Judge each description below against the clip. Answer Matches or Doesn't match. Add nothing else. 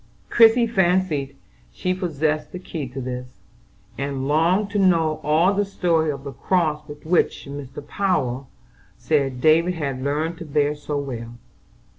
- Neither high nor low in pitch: Matches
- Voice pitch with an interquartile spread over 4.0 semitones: Matches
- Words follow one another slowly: Doesn't match